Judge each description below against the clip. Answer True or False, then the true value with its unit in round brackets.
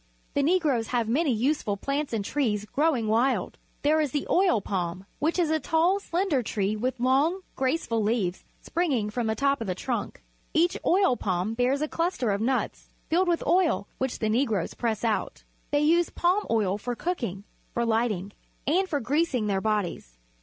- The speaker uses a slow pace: False (180 wpm)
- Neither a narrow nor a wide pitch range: False (6.6 semitones)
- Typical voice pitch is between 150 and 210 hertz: False (255 Hz)